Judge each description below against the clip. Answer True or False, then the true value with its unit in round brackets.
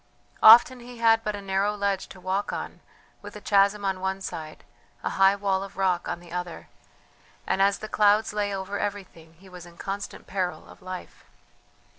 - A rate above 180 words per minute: True (190 wpm)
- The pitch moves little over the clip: True (1.7 semitones)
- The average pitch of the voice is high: True (195 Hz)